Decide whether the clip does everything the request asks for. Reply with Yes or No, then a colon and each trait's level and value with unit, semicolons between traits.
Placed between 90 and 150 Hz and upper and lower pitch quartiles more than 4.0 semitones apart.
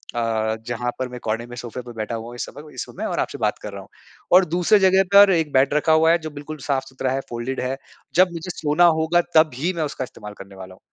Yes: low, 135 Hz; average, 5.3 semitones